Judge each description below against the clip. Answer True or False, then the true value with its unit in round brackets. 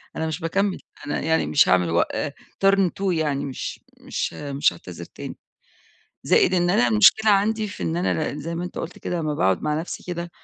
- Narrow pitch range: False (4.0 semitones)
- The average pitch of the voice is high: False (160 Hz)